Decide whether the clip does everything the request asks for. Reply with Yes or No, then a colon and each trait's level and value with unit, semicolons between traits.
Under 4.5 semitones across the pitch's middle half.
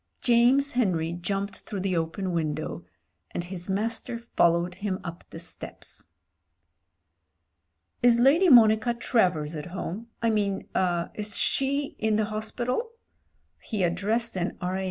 No: average, 4.8 semitones